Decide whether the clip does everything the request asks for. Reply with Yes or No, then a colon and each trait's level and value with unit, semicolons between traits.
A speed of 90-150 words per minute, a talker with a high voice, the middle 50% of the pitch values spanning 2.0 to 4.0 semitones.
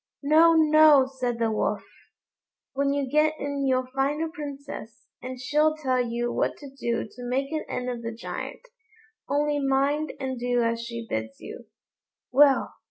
No: average, 165 wpm; very high, 270 Hz; average, 3.3 semitones